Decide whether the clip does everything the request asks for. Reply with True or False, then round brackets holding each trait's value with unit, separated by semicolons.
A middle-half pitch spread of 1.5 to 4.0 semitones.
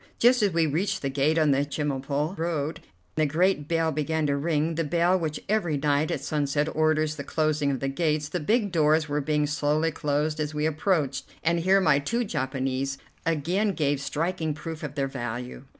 True (2.5 semitones)